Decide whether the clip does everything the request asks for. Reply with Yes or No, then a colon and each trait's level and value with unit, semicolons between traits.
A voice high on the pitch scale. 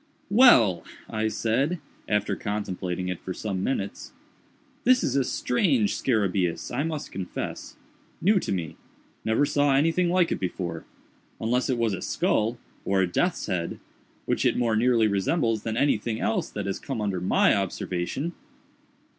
No: low, 110 Hz